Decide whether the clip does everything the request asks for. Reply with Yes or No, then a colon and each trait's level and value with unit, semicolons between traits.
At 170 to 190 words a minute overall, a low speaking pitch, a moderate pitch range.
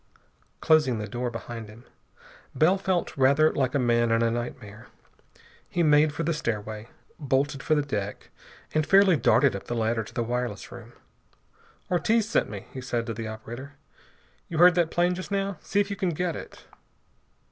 No: average, 180 wpm; low, 130 Hz; wide, 6.3 semitones